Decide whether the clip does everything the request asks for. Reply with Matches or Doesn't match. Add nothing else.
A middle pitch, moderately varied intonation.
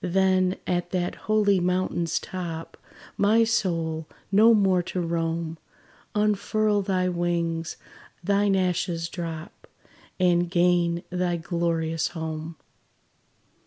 Doesn't match